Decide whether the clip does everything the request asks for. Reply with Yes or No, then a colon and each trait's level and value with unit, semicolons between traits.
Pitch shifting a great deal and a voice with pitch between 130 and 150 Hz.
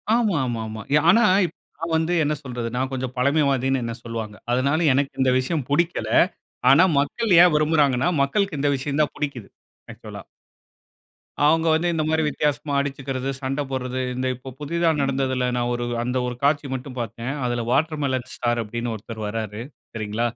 No: average, 3.7 semitones; low, 135 Hz